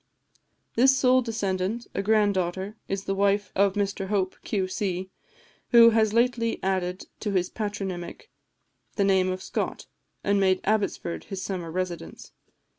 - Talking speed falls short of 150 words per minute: Yes, average, 140 wpm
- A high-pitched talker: Yes, high, 195 Hz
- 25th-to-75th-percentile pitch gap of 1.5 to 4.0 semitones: Yes, narrow, 2.5 semitones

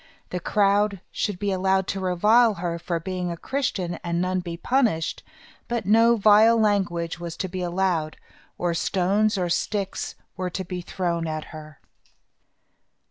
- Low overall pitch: No, medium, 185 Hz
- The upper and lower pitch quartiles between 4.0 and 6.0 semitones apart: No, average, 3.1 semitones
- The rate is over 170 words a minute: No, average, 155 wpm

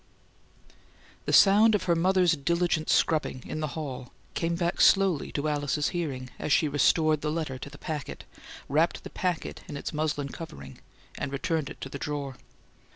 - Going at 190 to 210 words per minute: No, average, 170 wpm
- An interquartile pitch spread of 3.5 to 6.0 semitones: No, average, 3.1 semitones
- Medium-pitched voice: Yes, medium, 155 Hz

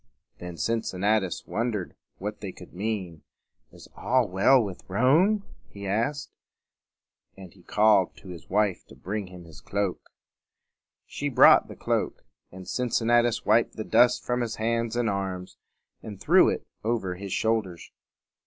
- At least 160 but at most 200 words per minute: No, average, 145 wpm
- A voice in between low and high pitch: No, low, 105 Hz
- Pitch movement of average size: Yes, average, 3.9 semitones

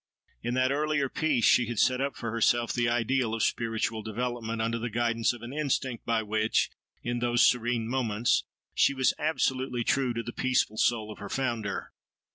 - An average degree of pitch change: No, narrow, 2.2 semitones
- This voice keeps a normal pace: Yes, average, 185 wpm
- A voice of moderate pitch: No, low, 120 Hz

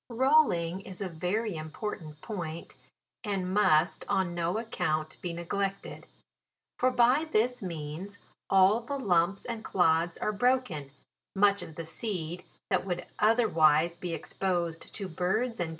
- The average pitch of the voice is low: No, medium, 185 Hz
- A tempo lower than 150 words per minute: Yes, average, 140 wpm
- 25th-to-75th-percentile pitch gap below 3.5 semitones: No, average, 4.4 semitones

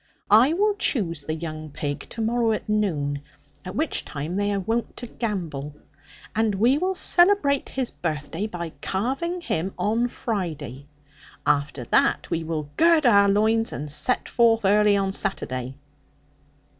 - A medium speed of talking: Yes, average, 150 wpm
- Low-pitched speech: No, high, 205 Hz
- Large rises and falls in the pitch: Yes, wide, 7.1 semitones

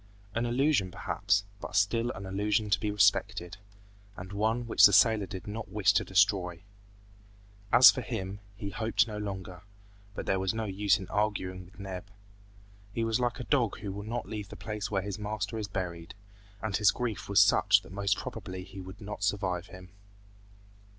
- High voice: No, low, 100 Hz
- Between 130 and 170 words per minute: No, average, 185 wpm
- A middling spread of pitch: No, narrow, 2.3 semitones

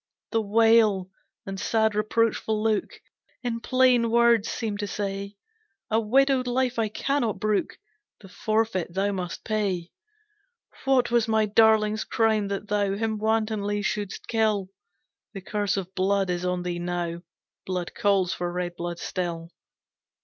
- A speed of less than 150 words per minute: Yes, average, 140 wpm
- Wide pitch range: No, average, 2.9 semitones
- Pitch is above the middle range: Yes, high, 210 Hz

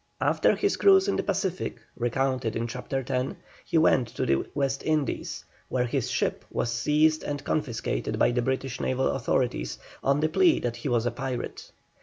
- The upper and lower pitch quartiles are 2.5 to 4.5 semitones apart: Yes, average, 3.7 semitones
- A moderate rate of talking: Yes, average, 180 wpm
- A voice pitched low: Yes, low, 130 Hz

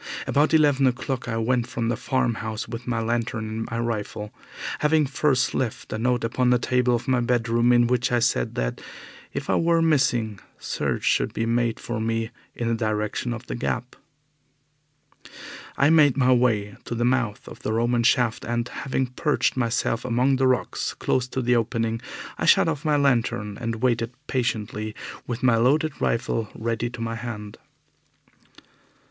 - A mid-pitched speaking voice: No, low, 120 Hz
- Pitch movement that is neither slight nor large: No, narrow, 2.0 semitones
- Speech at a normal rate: Yes, average, 175 wpm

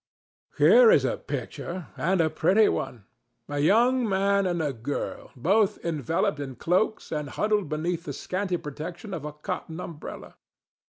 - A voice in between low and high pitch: Yes, medium, 165 Hz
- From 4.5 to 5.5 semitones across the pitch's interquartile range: Yes, average, 5.0 semitones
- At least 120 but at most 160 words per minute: Yes, average, 145 wpm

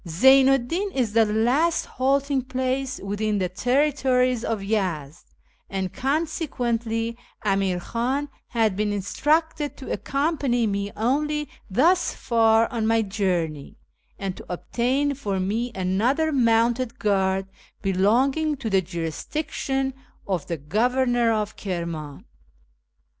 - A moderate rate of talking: No, slow, 120 wpm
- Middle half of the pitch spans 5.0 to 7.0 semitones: Yes, wide, 5.4 semitones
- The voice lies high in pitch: Yes, high, 230 Hz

